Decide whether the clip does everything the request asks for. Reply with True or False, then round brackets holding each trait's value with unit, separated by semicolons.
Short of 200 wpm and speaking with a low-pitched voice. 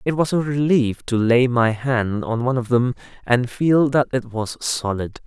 False (205 wpm; 125 Hz)